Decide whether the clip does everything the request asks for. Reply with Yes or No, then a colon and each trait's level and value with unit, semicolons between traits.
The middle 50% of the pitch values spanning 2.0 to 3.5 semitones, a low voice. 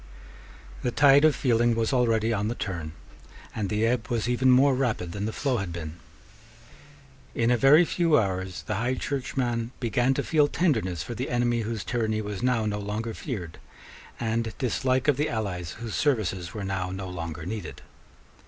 No: average, 4.2 semitones; low, 115 Hz